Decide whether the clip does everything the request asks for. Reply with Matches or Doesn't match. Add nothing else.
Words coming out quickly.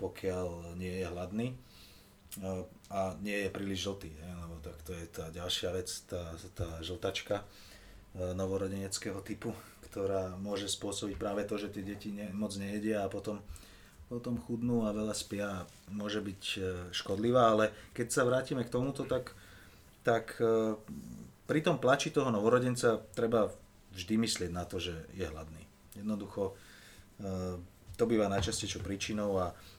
Doesn't match